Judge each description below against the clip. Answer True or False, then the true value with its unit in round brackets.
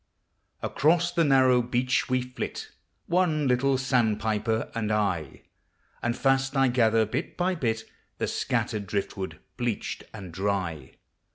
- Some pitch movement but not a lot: True (4.0 semitones)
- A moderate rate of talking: False (125 wpm)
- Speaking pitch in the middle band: False (120 Hz)